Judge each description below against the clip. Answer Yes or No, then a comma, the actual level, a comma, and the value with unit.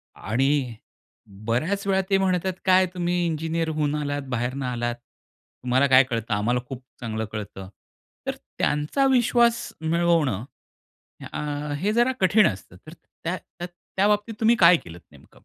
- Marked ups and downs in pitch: Yes, wide, 7.3 semitones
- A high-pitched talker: No, medium, 150 Hz